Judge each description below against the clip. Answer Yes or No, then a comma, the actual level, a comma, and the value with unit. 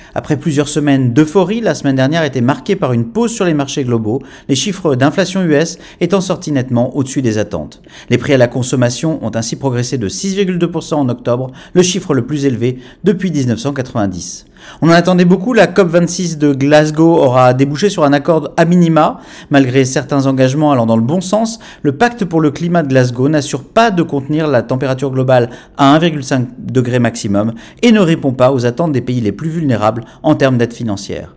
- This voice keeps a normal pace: Yes, average, 195 wpm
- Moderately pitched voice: Yes, medium, 145 Hz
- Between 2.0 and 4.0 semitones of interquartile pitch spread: No, average, 4.9 semitones